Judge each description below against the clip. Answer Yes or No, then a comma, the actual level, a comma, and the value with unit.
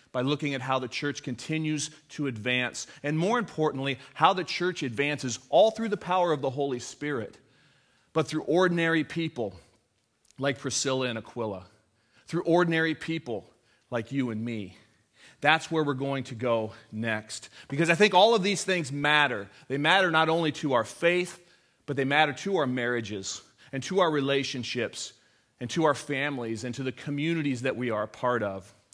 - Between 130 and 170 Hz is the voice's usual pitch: Yes, medium, 140 Hz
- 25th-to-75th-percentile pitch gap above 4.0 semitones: Yes, average, 4.6 semitones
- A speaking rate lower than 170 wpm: No, average, 175 wpm